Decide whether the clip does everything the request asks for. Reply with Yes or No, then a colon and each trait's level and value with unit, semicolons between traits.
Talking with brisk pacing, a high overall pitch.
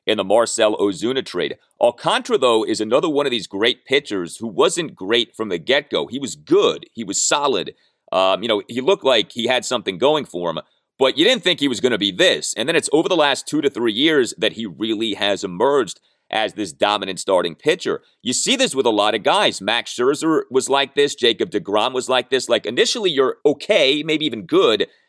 Yes: fast, 225 wpm; very high, 335 Hz